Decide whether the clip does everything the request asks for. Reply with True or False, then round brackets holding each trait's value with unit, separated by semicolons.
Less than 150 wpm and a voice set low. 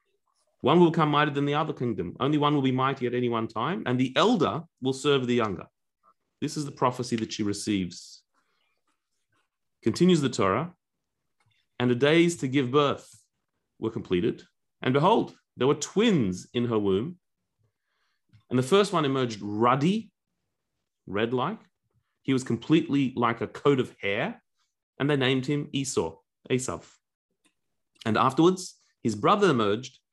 False (155 wpm; 130 Hz)